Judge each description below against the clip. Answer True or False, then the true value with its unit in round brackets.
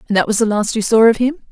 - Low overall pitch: False (220 Hz)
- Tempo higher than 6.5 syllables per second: True (7.0 syllables/s)